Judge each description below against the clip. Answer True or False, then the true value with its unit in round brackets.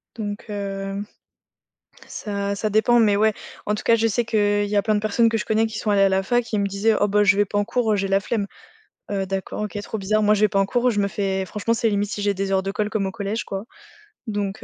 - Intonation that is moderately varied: False (1.6 semitones)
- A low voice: False (205 Hz)